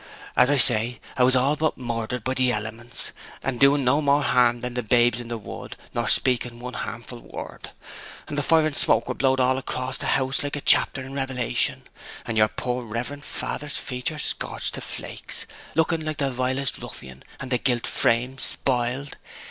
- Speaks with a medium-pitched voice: No, low, 125 Hz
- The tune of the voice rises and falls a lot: No, narrow, 2.4 semitones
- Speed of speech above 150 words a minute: Yes, average, 190 wpm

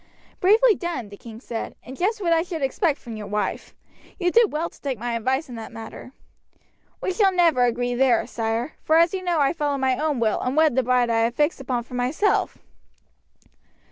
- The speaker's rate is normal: No, fast, 210 wpm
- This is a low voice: No, very high, 265 Hz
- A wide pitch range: Yes, wide, 5.9 semitones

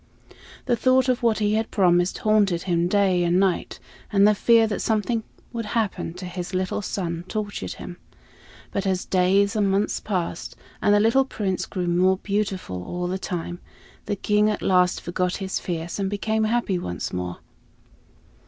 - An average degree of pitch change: Yes, average, 3.0 semitones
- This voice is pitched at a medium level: No, high, 195 Hz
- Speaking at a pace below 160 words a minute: No, average, 170 wpm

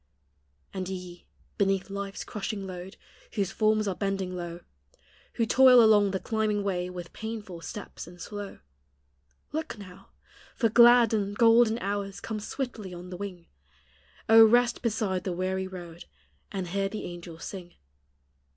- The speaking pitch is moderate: No, high, 195 Hz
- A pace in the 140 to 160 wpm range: Yes, average, 150 wpm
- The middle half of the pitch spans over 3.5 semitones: No, average, 3.2 semitones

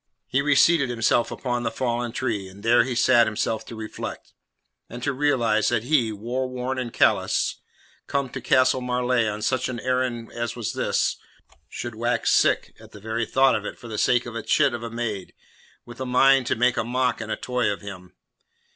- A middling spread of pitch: No, narrow, 2.3 semitones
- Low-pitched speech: Yes, low, 120 Hz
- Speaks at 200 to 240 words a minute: Yes, fast, 205 wpm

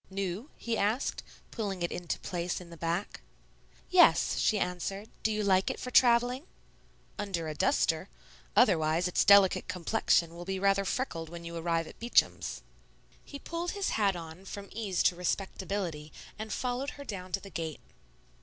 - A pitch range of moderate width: Yes, average, 4.2 semitones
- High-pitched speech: Yes, high, 195 Hz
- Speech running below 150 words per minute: No, average, 165 wpm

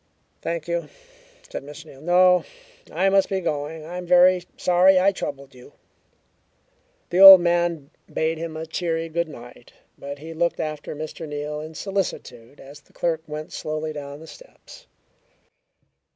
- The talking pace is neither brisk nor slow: Yes, average, 155 wpm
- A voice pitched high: No, medium, 160 Hz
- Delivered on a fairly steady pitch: No, average, 3.0 semitones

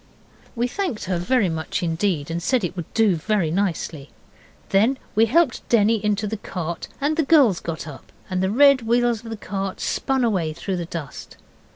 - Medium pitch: No, high, 205 Hz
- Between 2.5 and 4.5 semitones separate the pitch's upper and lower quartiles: No, wide, 5.6 semitones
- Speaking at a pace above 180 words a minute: Yes, average, 190 wpm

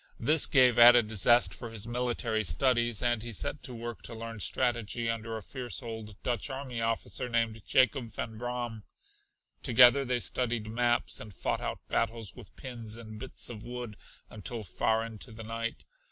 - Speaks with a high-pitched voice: No, low, 115 Hz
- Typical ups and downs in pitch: No, narrow, 1.6 semitones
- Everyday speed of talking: Yes, average, 170 wpm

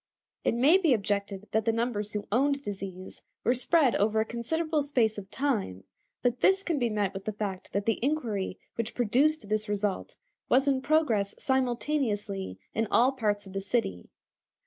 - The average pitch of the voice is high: Yes, high, 225 Hz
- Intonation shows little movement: No, average, 4.7 semitones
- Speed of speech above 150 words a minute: Yes, average, 175 wpm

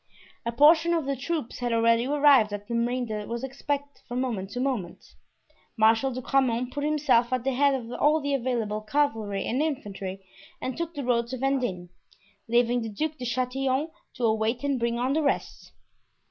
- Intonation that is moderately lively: Yes, average, 3.4 semitones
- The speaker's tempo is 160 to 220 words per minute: Yes, average, 185 wpm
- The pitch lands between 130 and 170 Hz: No, very high, 250 Hz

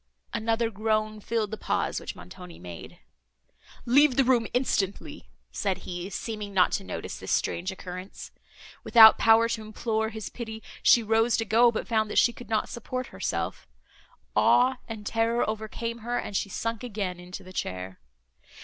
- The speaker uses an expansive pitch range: No, average, 2.8 semitones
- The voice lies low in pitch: No, high, 220 Hz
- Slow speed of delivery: No, average, 165 wpm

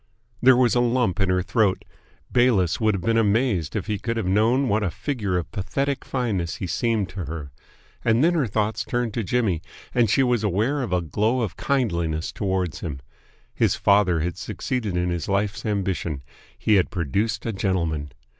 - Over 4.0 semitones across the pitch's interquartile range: Yes, average, 4.8 semitones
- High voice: No, low, 105 Hz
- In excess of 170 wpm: Yes, average, 190 wpm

